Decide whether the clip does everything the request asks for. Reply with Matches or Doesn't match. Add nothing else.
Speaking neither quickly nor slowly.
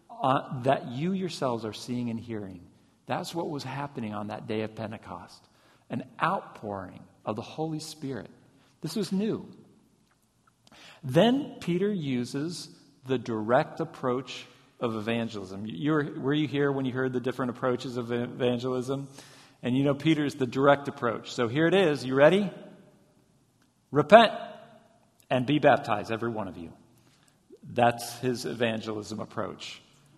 Matches